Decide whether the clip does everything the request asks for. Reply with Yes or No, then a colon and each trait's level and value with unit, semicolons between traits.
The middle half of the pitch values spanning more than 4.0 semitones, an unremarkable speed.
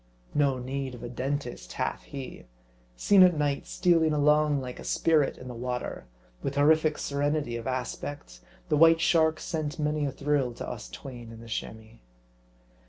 No: average, 3.6 semitones; average, 170 wpm